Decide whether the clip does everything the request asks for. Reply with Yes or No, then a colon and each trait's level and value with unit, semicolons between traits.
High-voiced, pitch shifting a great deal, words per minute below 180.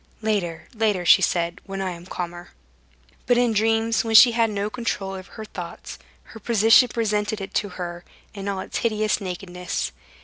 No: high, 205 Hz; average, 3.4 semitones; average, 170 wpm